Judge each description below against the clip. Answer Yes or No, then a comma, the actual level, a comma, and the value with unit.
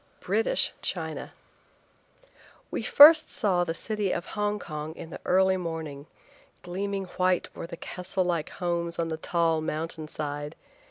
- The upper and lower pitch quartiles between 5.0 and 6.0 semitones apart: No, average, 3.0 semitones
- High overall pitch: No, medium, 175 Hz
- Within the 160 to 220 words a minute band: No, average, 145 wpm